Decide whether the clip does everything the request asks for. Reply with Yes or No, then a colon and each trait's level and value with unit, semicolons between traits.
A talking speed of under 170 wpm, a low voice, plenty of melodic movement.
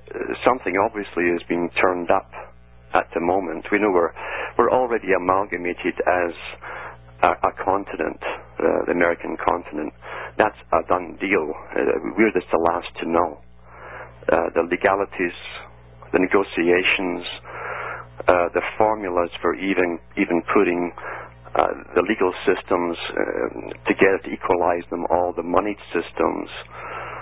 Yes: slow, 135 wpm; very low, 85 Hz; wide, 6.4 semitones